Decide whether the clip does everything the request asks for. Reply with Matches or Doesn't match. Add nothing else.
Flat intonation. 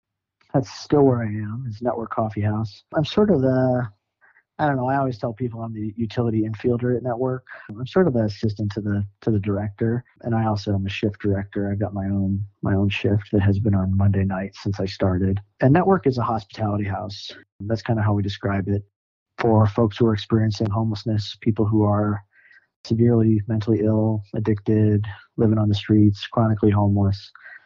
Matches